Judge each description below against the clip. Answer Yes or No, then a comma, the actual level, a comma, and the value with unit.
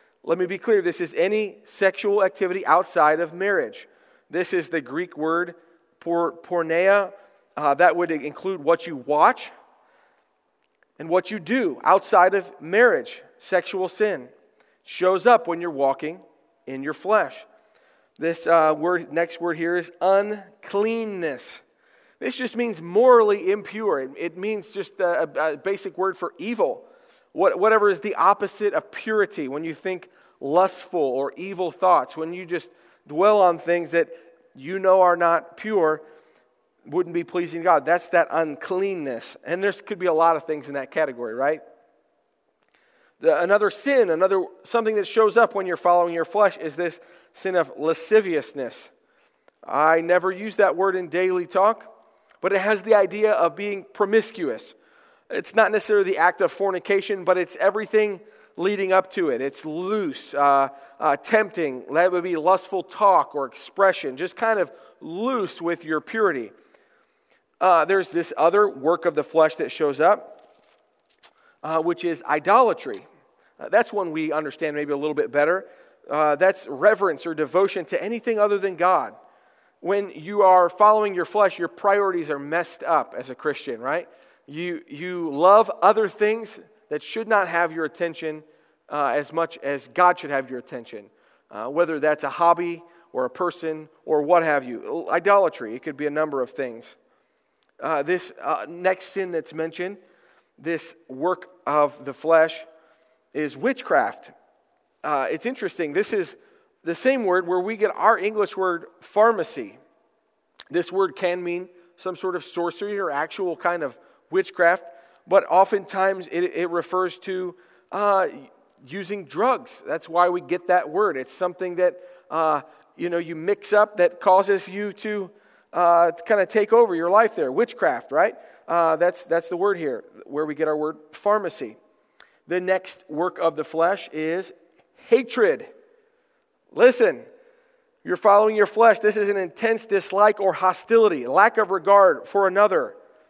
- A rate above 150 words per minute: Yes, average, 160 wpm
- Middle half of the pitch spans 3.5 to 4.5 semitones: Yes, average, 3.9 semitones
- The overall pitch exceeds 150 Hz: Yes, medium, 185 Hz